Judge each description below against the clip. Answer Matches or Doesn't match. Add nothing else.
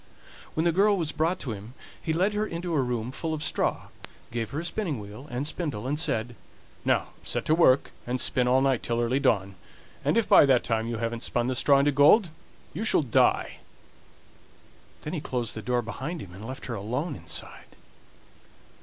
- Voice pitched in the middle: Doesn't match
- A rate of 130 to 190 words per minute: Doesn't match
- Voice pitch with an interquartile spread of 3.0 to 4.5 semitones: Doesn't match